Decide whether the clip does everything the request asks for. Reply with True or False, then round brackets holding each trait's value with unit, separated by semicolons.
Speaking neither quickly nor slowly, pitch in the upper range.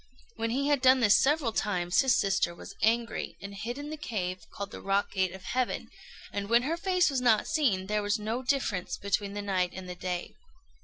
False (215 wpm; 210 Hz)